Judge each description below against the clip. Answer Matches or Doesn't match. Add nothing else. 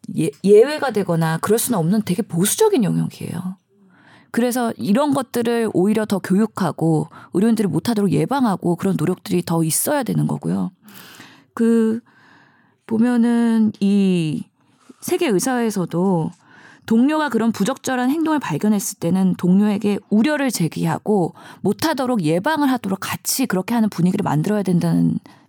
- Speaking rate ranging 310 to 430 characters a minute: Matches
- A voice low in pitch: Doesn't match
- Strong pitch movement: Doesn't match